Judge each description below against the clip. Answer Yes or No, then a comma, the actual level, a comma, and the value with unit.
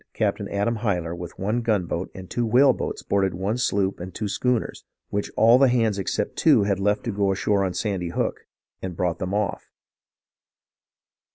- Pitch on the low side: Yes, low, 100 Hz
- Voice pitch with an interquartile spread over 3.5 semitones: No, average, 3.1 semitones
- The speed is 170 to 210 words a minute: Yes, average, 180 wpm